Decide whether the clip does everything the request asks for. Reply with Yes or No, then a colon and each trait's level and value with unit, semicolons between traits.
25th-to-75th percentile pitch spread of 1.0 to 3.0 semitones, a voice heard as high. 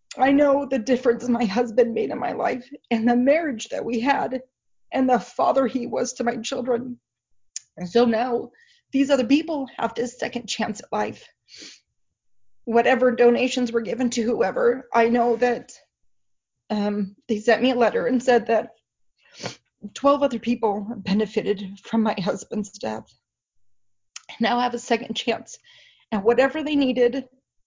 Yes: narrow, 2.6 semitones; high, 240 Hz